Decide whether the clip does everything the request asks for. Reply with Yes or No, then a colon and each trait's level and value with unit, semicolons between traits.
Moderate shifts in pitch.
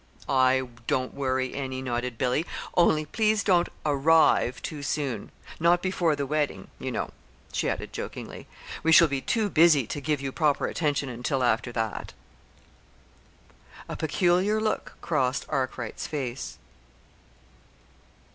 Yes: average, 4.0 semitones